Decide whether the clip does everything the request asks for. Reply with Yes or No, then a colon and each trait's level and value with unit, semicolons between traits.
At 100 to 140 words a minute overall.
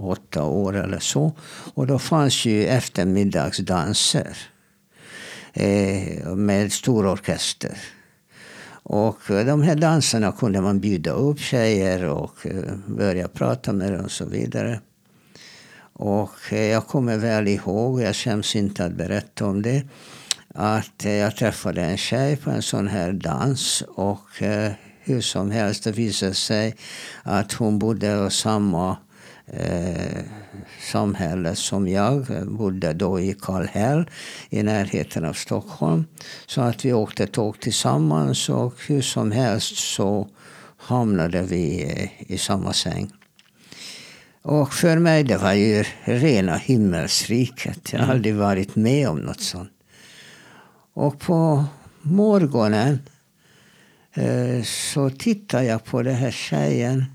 Yes: average, 130 wpm